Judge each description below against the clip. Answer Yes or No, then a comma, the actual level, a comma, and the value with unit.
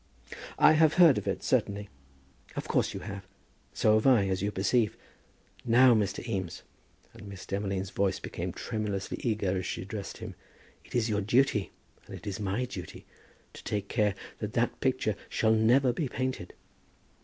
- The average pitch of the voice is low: Yes, low, 105 Hz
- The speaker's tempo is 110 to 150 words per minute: No, average, 170 wpm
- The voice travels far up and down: No, average, 3.8 semitones